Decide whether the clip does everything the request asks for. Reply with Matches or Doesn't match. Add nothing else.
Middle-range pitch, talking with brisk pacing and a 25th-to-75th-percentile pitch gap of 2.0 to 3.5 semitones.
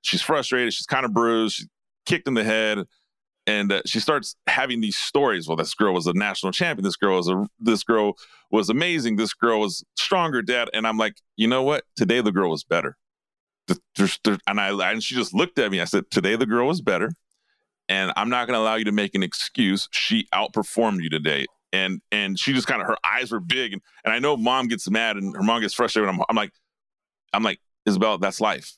Doesn't match